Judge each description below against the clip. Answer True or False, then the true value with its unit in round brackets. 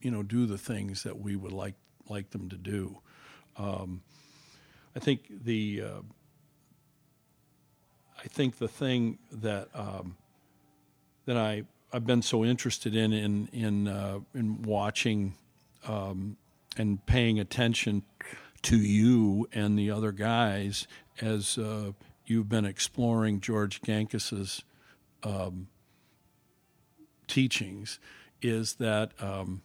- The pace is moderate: False (115 wpm)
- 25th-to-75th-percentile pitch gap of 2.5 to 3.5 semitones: True (2.8 semitones)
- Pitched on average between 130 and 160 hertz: False (110 Hz)